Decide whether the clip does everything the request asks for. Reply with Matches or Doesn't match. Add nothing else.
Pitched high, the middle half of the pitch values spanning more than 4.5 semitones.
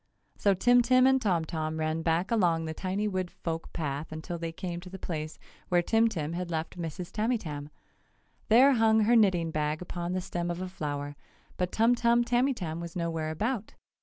Doesn't match